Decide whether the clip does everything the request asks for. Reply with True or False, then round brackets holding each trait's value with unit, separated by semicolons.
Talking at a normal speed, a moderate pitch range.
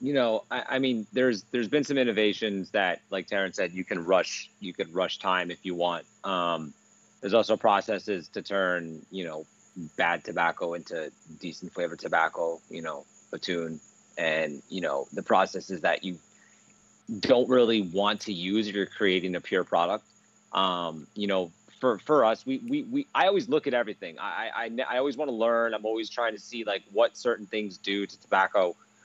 True (190 wpm; 4.5 semitones)